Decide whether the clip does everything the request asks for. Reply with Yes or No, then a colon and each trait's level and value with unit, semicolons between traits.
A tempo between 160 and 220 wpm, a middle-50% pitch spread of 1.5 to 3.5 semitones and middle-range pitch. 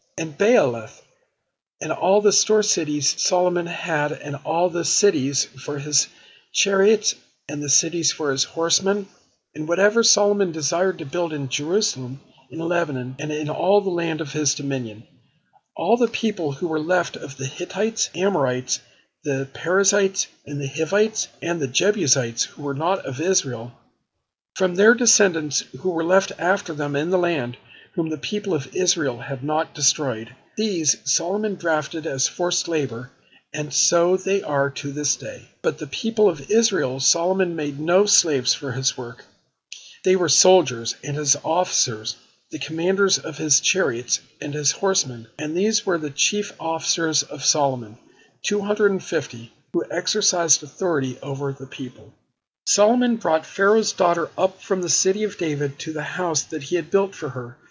No: average, 165 wpm; average, 5.3 semitones; medium, 160 Hz